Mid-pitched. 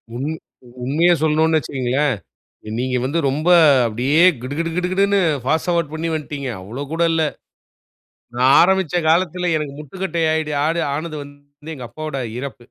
Yes: medium, 155 Hz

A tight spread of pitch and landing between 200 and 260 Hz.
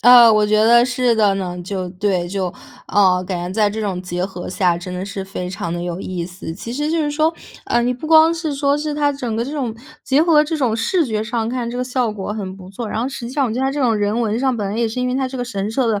No: average, 5.1 semitones; high, 225 Hz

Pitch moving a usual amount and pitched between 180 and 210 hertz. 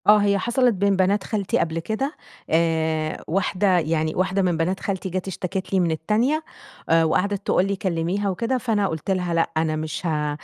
Yes: average, 3.7 semitones; medium, 185 Hz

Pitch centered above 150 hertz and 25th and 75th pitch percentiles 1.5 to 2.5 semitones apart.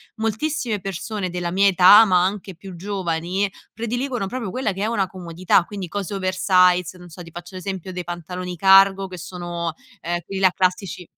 Yes: medium, 185 Hz; narrow, 2.1 semitones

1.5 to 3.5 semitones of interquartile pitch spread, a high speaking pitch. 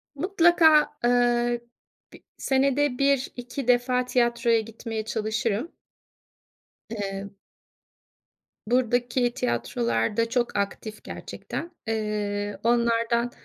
Yes: narrow, 2.6 semitones; high, 235 Hz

